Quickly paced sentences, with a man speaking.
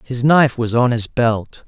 Yes: fast, 215 wpm; male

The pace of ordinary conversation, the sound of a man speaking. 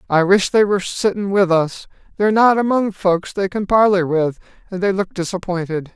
Yes: average, 190 wpm; male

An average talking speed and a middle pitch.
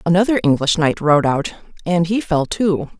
Yes: average, 180 wpm; medium, 170 Hz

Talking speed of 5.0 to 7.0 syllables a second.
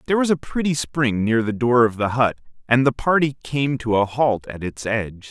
Yes: 5.2 syllables/s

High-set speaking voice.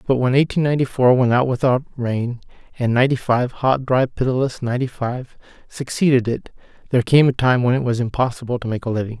No: low, 125 Hz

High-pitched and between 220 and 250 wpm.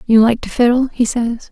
Yes: high, 235 Hz; fast, 235 wpm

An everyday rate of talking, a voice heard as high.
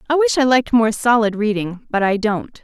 No: fast, 225 wpm; high, 230 Hz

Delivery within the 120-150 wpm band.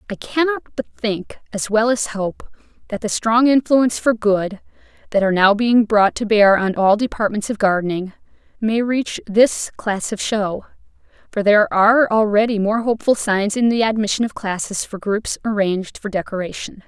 No: average, 175 wpm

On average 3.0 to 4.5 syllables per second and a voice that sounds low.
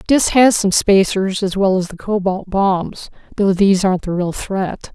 No: 4.4 syllables/s; high, 195 Hz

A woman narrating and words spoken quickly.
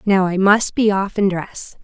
Yes: female; fast, 230 wpm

